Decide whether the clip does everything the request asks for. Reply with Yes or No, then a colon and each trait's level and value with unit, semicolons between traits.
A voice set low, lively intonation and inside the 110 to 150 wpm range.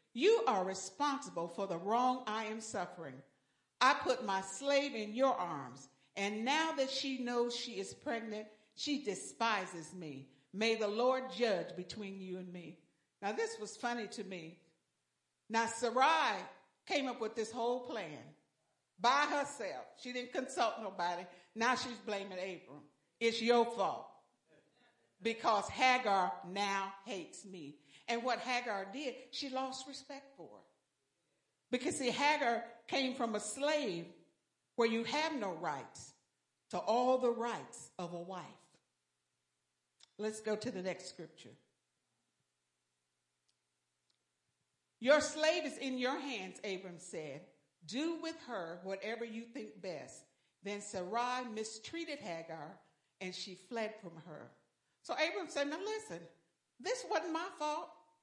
No: high, 215 Hz; wide, 6.7 semitones; slow, 135 wpm